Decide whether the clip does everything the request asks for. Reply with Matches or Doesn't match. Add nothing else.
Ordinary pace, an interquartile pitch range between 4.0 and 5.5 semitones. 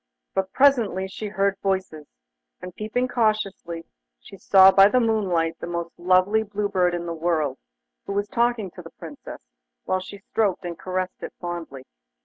Doesn't match